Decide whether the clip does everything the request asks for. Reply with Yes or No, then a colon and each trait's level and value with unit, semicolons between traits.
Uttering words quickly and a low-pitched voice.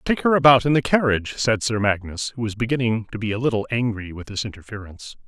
Yes: fast, 225 wpm; low, 115 Hz